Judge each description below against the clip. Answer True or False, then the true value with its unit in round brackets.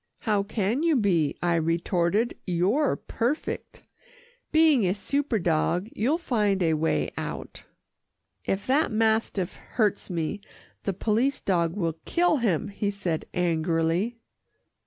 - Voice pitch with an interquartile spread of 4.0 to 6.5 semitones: True (5.5 semitones)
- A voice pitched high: True (200 Hz)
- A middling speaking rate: False (125 wpm)